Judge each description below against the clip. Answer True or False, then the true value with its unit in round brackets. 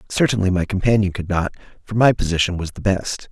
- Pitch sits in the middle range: False (95 Hz)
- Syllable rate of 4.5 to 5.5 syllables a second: False (6.1 syllables/s)